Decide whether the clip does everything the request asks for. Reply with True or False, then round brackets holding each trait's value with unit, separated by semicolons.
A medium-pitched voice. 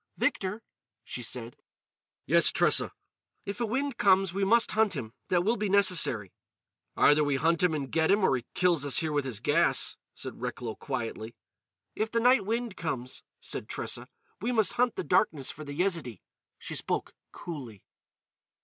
True (170 Hz)